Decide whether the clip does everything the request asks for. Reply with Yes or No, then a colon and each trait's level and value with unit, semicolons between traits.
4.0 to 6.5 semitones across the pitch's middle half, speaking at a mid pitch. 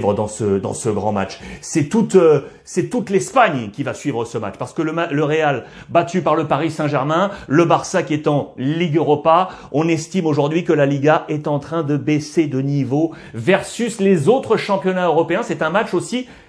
No: average, 3.6 semitones; medium, 160 Hz